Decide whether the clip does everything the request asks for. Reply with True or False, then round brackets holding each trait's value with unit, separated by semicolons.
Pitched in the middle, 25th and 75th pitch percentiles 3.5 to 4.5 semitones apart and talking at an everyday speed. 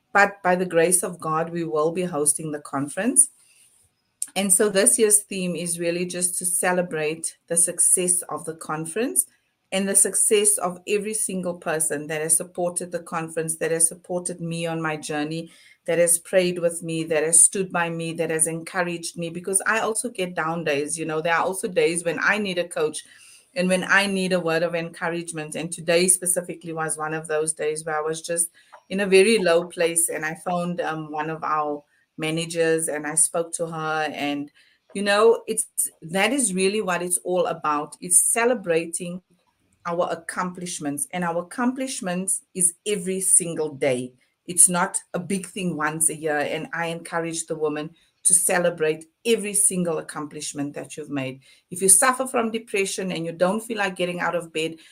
False (175 Hz; 2.8 semitones; 190 wpm)